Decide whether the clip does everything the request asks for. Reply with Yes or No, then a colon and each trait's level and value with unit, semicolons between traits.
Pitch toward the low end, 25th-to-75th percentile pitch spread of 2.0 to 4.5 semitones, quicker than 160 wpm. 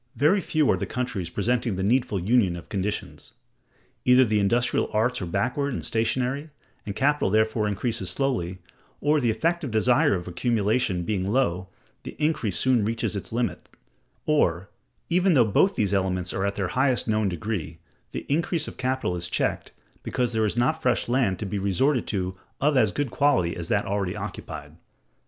No: low, 110 Hz; average, 5.2 semitones; average, 175 wpm